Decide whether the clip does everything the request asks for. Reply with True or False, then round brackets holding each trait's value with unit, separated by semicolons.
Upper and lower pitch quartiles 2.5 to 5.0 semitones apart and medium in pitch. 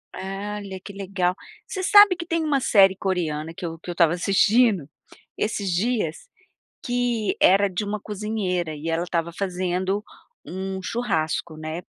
False (3.4 semitones; 195 Hz)